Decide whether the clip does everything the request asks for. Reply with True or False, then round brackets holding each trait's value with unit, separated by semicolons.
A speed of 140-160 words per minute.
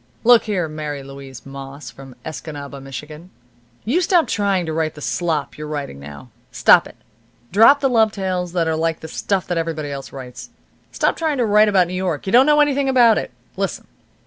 False (200 wpm)